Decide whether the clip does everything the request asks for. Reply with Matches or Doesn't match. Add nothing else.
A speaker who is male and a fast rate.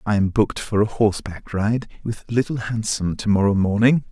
Doesn't match